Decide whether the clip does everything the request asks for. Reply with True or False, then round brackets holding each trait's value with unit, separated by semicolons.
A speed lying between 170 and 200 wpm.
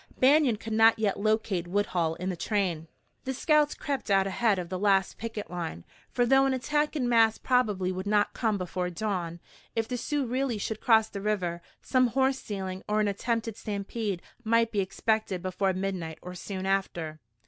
True (185 wpm)